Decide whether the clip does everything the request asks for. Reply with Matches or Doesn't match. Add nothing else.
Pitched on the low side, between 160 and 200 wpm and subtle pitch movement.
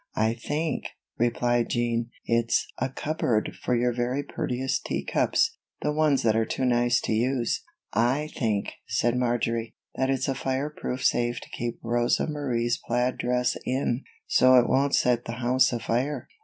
Matches